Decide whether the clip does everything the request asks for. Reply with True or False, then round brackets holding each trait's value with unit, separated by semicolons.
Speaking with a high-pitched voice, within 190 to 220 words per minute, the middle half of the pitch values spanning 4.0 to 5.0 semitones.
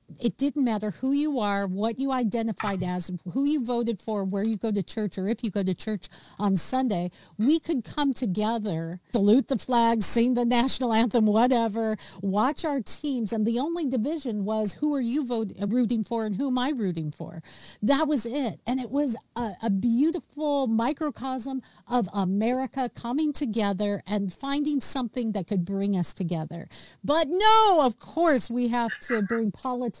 False (230 Hz; 180 wpm; 4.4 semitones)